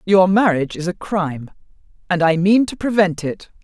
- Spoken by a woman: Yes, female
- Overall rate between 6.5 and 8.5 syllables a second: No, 5.3 syllables/s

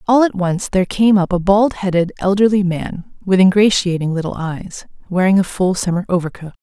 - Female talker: Yes, female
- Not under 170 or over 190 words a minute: Yes, average, 180 wpm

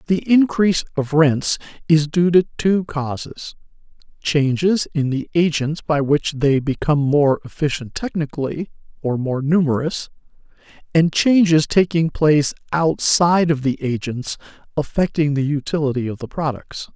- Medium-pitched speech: Yes, medium, 150 Hz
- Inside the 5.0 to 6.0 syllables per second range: No, 4.6 syllables/s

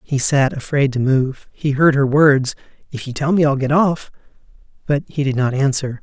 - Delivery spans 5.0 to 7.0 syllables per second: No, 4.8 syllables/s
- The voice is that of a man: Yes, male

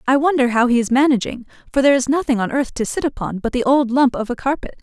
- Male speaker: No, female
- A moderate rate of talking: No, fast, 275 wpm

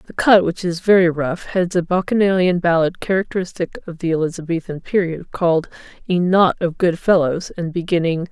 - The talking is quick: No, average, 165 wpm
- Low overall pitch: No, medium, 175 Hz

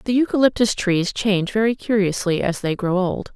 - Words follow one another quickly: No, average, 180 wpm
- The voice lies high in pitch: Yes, high, 205 Hz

